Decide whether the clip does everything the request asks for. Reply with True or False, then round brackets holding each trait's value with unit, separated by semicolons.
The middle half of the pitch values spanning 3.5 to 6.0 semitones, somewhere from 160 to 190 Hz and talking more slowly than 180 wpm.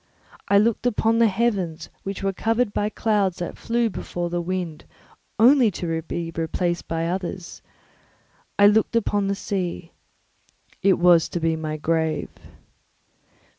True (3.8 semitones; 185 Hz; 140 wpm)